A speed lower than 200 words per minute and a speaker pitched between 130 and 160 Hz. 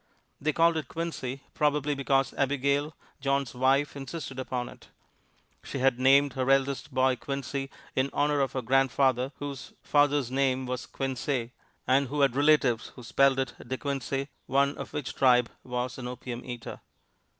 Yes: average, 160 wpm; low, 135 Hz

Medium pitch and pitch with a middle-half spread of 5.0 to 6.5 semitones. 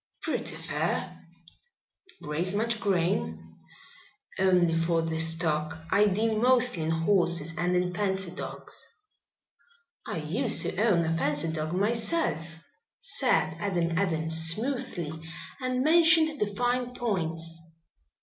Yes: medium, 180 Hz; wide, 5.6 semitones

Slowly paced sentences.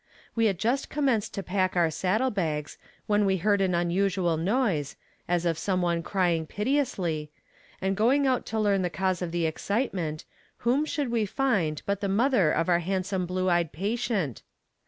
No: average, 175 wpm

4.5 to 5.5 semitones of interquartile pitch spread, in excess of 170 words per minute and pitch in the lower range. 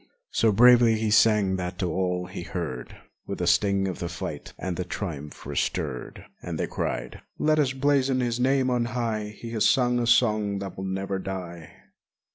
Yes: average, 5.0 semitones; average, 185 wpm; low, 100 Hz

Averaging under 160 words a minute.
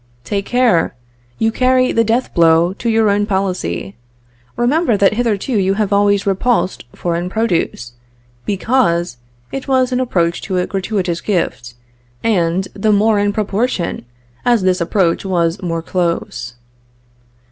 Yes: slow, 135 wpm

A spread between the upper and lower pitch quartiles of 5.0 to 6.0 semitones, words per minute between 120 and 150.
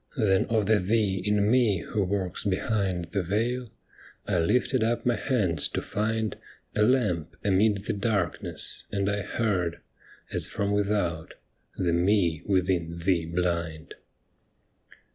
No: average, 3.5 semitones; average, 145 wpm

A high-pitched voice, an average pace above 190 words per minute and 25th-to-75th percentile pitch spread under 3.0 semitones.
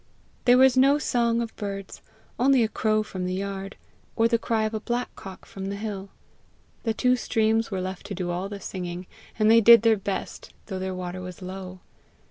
No: high, 205 Hz; average, 200 wpm; average, 3.4 semitones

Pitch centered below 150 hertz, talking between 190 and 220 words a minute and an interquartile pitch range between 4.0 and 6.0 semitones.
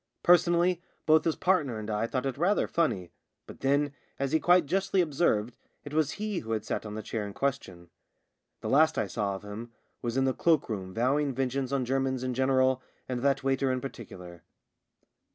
Yes: low, 135 Hz; average, 200 wpm; average, 5.1 semitones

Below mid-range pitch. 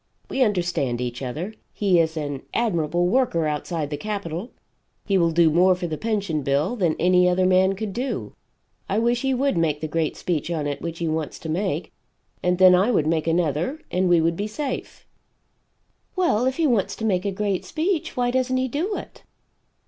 No: medium, 180 Hz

